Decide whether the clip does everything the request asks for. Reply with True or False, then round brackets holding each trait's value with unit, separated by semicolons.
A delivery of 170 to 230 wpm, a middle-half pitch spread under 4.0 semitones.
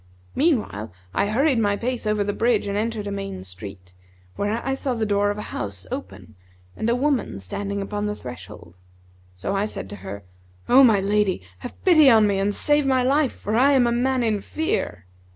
False (205 wpm; 4.3 semitones)